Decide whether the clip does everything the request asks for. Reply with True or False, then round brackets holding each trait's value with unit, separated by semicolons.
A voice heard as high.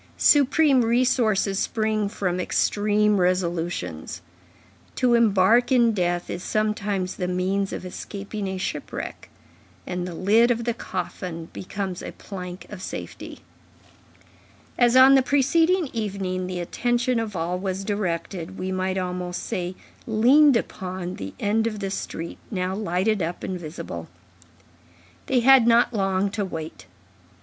True (195 Hz)